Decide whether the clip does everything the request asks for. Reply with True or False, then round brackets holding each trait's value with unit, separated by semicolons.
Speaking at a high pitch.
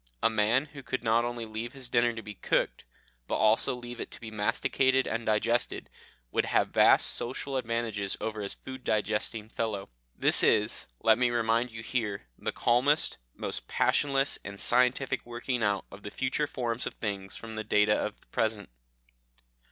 False (115 Hz)